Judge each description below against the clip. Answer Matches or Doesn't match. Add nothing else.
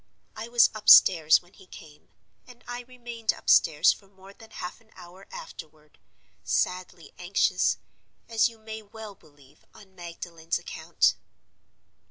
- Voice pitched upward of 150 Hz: Matches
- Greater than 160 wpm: Doesn't match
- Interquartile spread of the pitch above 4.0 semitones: Matches